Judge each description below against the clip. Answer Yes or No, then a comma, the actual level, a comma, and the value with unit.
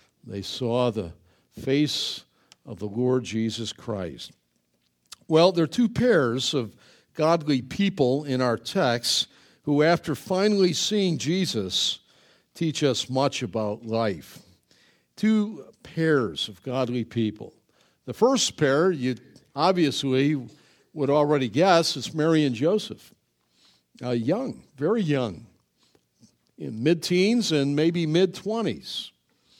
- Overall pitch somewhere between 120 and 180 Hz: Yes, medium, 140 Hz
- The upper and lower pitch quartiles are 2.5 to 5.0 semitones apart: No, wide, 5.5 semitones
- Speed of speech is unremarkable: No, slow, 120 wpm